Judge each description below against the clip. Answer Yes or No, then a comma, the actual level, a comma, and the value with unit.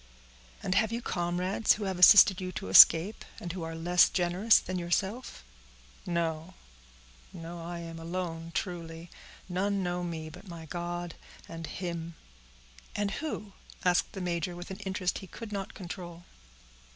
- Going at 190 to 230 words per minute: No, average, 145 wpm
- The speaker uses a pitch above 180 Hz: No, medium, 175 Hz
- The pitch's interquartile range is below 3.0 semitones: Yes, narrow, 2.4 semitones